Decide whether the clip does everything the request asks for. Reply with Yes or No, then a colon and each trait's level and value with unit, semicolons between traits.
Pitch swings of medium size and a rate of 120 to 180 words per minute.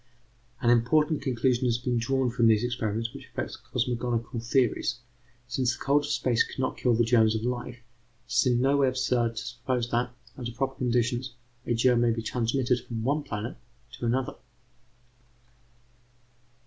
No: narrow, 1.6 semitones; average, 170 wpm